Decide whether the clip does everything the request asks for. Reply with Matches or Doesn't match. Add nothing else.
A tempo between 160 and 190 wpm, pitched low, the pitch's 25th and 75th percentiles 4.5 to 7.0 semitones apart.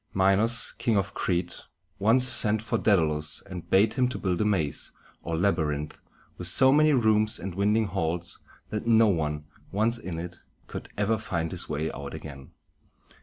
Matches